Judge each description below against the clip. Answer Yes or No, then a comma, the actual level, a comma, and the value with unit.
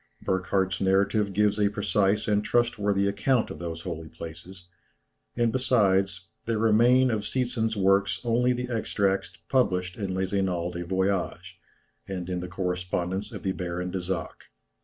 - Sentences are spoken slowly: No, average, 150 wpm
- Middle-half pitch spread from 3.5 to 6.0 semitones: No, average, 2.9 semitones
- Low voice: Yes, very low, 95 Hz